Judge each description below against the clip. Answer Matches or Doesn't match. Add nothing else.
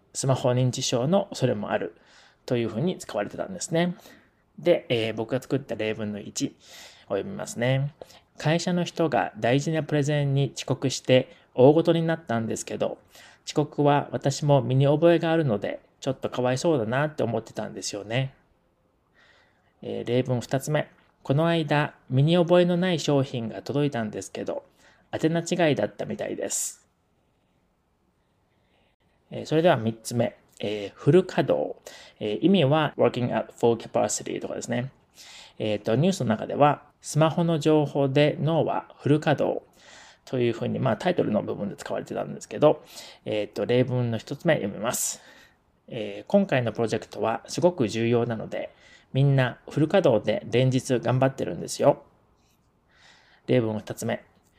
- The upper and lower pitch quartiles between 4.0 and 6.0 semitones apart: Matches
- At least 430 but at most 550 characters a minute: Doesn't match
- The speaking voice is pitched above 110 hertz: Matches